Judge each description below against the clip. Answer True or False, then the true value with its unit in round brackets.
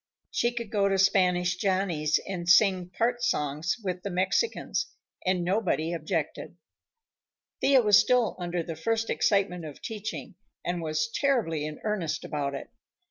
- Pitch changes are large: False (4.2 semitones)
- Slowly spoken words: False (145 wpm)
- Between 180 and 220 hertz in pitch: True (185 Hz)